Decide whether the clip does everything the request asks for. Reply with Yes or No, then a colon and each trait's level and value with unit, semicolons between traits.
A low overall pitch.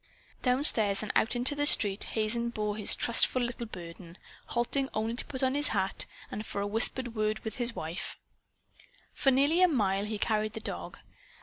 No: high, 225 Hz